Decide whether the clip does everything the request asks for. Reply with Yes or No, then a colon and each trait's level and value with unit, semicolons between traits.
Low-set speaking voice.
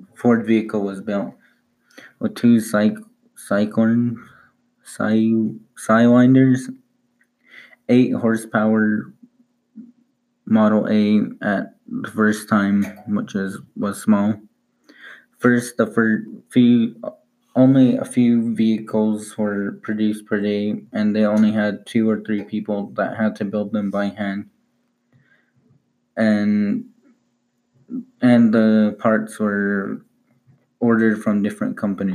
Yes: low, 115 Hz